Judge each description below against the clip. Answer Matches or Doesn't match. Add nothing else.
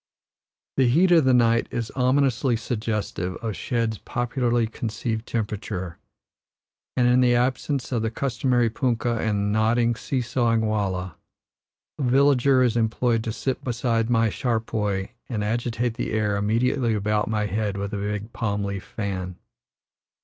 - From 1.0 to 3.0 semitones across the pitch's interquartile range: Matches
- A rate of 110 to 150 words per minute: Matches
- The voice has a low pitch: Matches